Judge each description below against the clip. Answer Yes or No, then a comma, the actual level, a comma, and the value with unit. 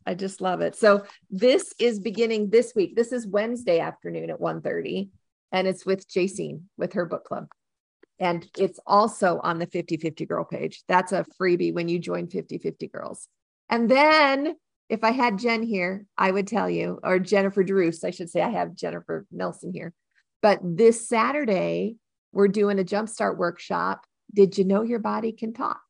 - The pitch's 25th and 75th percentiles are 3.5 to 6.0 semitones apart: Yes, average, 3.9 semitones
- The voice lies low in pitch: No, high, 200 Hz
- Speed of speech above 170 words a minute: Yes, average, 185 wpm